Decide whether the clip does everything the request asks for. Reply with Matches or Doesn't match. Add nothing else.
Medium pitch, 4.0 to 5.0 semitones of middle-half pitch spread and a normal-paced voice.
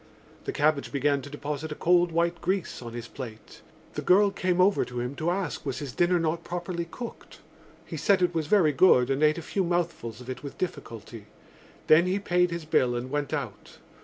Doesn't match